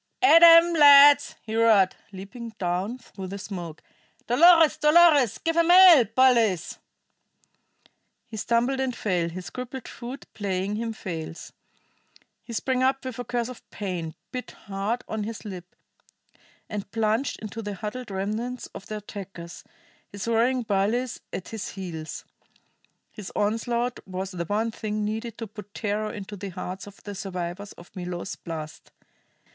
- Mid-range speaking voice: No, high, 215 Hz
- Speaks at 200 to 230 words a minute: No, average, 150 wpm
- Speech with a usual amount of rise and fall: Yes, average, 4.3 semitones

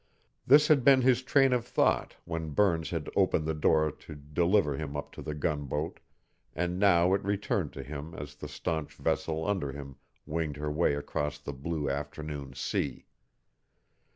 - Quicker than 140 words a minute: Yes, average, 170 wpm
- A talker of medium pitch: No, very low, 80 Hz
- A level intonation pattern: No, average, 3.6 semitones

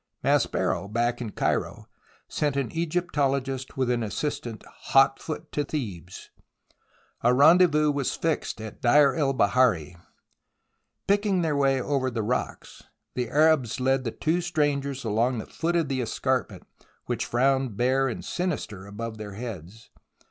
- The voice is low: Yes, low, 130 Hz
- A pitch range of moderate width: Yes, average, 4.4 semitones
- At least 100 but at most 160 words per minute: Yes, average, 140 wpm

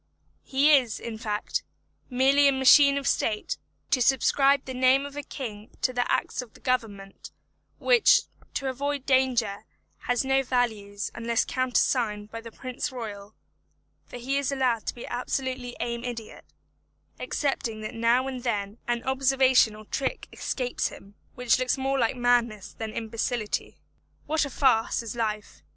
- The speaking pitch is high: Yes, high, 245 Hz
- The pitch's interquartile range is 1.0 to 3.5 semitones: Yes, average, 2.9 semitones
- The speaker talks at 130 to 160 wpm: Yes, average, 155 wpm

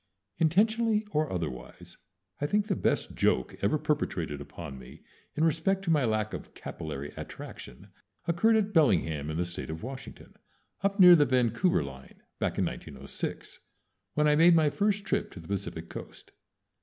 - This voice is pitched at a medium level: Yes, medium, 145 Hz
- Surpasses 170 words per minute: No, average, 165 wpm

